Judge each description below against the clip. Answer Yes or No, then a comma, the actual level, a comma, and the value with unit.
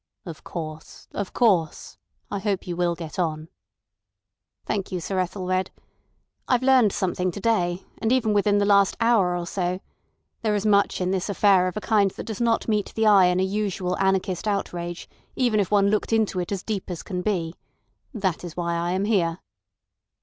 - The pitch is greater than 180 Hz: Yes, high, 190 Hz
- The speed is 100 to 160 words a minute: No, average, 185 wpm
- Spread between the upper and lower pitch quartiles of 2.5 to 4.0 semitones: Yes, average, 2.8 semitones